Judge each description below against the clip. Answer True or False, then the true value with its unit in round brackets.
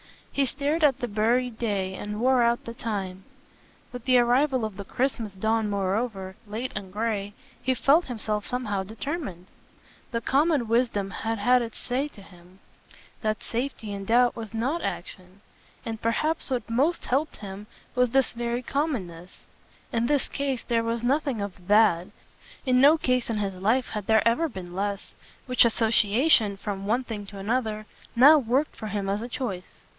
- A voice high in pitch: True (230 Hz)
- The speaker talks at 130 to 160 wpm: False (170 wpm)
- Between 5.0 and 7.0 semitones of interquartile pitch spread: False (3.8 semitones)